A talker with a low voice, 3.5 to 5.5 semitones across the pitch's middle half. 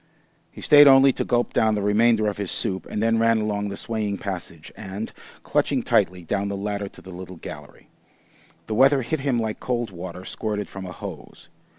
No: low, 105 Hz; average, 2.9 semitones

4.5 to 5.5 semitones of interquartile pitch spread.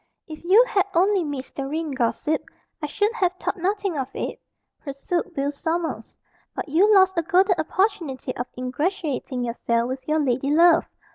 Yes: average, 5.2 semitones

